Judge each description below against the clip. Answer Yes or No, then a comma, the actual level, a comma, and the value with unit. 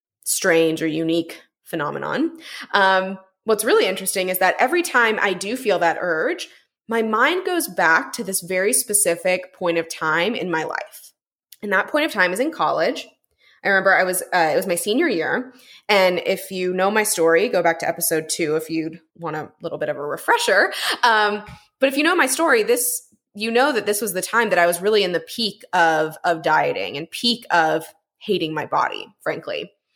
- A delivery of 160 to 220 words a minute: Yes, average, 200 wpm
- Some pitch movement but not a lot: No, wide, 5.8 semitones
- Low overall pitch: No, high, 190 Hz